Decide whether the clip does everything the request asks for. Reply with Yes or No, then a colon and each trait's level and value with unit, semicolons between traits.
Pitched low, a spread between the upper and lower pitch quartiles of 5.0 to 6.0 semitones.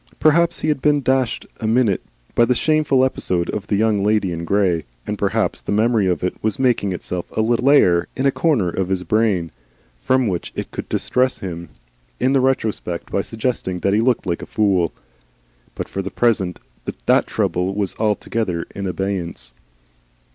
Yes: low, 105 Hz; wide, 5.6 semitones